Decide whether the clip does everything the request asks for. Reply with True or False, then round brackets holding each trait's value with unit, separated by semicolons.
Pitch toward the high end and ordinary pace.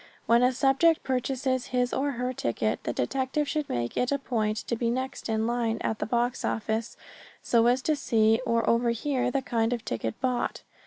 True (245 Hz; 195 wpm)